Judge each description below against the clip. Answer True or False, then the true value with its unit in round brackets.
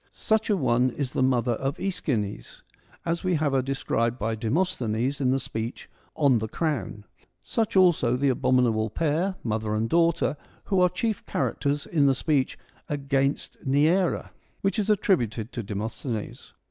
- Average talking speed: True (170 wpm)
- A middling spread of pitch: False (6.2 semitones)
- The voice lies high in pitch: False (135 Hz)